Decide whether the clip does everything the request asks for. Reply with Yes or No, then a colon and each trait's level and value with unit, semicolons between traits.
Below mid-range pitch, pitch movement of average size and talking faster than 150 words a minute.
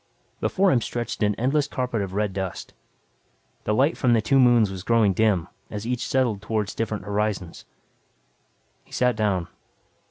Yes: low, 110 Hz; average, 3.4 semitones; average, 160 wpm